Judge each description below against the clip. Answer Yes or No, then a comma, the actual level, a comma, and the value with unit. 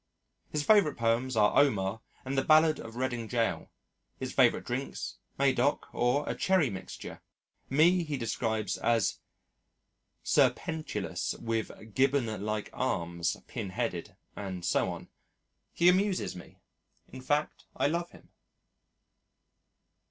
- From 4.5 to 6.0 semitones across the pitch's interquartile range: Yes, wide, 5.5 semitones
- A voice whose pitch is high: No, low, 125 Hz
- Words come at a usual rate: No, slow, 120 wpm